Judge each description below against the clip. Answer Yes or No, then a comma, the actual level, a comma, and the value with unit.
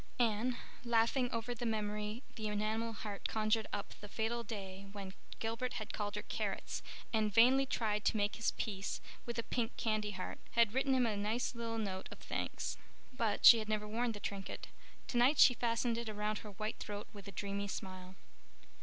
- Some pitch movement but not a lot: No, narrow, 2.1 semitones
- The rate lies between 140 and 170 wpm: No, average, 190 wpm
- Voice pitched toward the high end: Yes, high, 220 Hz